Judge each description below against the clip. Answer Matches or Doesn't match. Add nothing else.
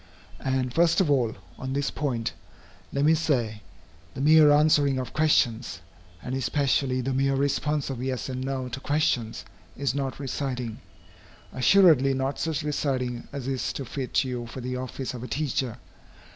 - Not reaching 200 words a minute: Matches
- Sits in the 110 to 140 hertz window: Matches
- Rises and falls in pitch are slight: Matches